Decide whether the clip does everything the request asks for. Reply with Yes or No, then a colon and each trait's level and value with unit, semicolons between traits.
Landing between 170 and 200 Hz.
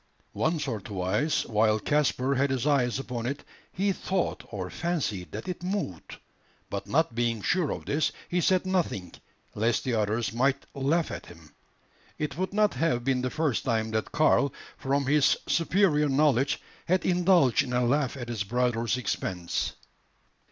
No: low, 135 Hz